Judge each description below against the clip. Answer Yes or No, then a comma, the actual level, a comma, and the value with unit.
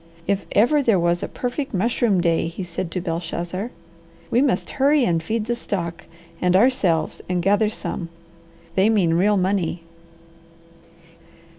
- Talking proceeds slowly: No, average, 145 wpm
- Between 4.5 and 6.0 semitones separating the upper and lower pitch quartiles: Yes, average, 4.8 semitones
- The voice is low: No, high, 190 Hz